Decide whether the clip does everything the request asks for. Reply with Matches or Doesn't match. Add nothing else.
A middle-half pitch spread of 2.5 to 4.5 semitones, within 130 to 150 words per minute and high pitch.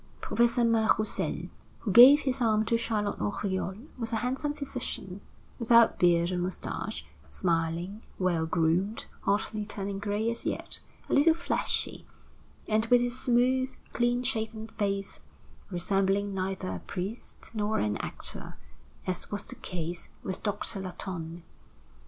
Matches